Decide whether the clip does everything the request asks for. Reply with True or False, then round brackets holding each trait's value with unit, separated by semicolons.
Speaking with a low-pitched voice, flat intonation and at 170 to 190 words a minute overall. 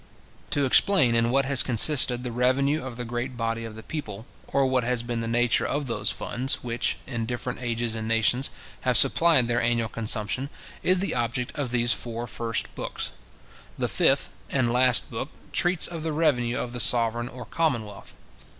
True (120 Hz; 2.3 semitones; 185 wpm)